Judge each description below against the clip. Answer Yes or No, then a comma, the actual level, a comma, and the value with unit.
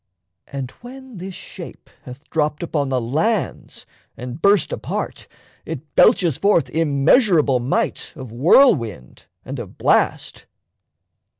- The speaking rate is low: Yes, slow, 115 wpm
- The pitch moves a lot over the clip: Yes, wide, 7.2 semitones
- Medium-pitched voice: Yes, medium, 155 Hz